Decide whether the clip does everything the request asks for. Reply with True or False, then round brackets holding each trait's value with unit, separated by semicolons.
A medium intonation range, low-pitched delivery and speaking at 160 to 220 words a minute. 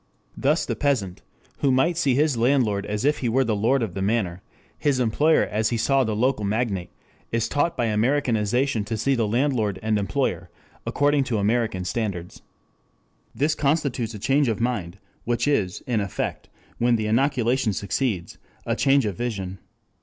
True (4.4 semitones; 115 Hz; 170 wpm)